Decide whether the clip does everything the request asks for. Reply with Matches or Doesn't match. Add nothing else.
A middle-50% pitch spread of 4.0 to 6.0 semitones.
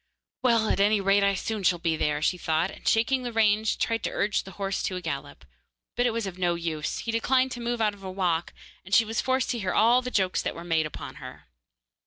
Matches